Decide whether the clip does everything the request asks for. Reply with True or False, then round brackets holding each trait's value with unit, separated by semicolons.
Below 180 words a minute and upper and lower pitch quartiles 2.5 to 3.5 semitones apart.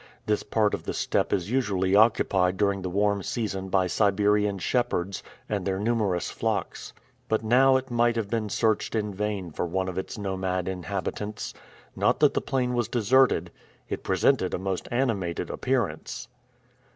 True (165 wpm; 3.2 semitones)